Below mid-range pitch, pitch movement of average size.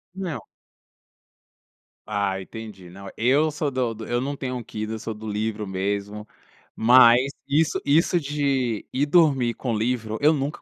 Yes: low, 120 Hz; average, 4.8 semitones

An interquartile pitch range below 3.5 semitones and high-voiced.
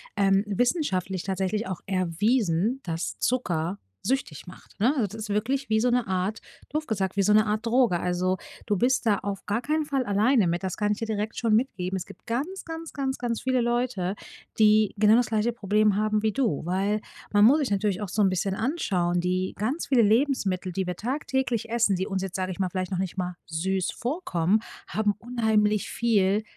No: average, 4.1 semitones; high, 210 Hz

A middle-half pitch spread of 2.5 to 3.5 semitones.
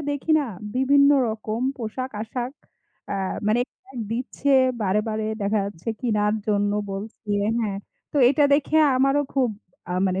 No: average, 4.1 semitones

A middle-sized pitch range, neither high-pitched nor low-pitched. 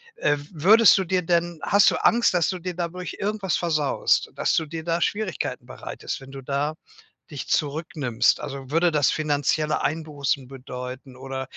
Yes: average, 4.2 semitones; medium, 155 Hz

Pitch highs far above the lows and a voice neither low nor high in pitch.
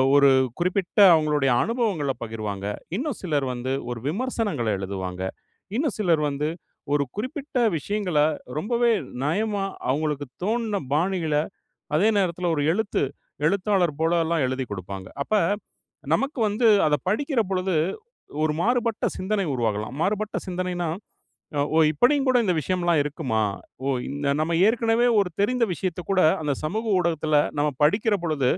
Yes: wide, 6.6 semitones; medium, 175 Hz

